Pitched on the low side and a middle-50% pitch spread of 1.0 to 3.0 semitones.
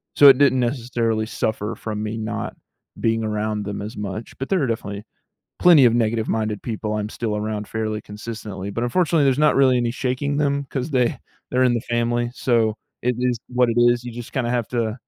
Yes: low, 115 Hz; average, 2.7 semitones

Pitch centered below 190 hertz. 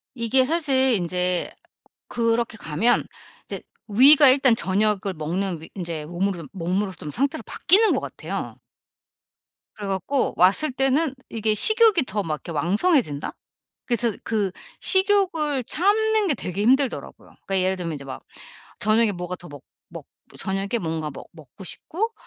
No: high, 210 Hz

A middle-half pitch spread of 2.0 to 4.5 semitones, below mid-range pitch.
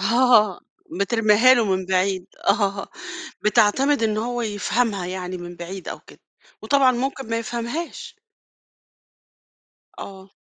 No: average, 4.2 semitones; high, 215 Hz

